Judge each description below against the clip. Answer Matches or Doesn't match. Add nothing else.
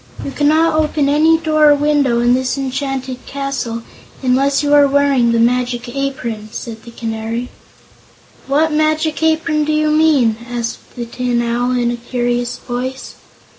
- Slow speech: Doesn't match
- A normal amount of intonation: Matches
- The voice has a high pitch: Matches